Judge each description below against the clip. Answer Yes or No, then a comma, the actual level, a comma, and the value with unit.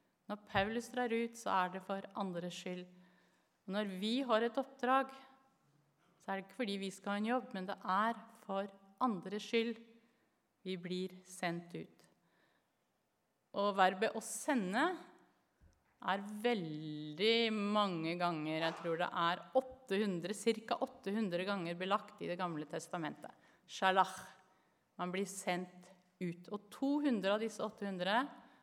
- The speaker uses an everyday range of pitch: Yes, average, 4.0 semitones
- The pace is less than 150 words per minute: Yes, average, 140 wpm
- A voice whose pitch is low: No, high, 200 Hz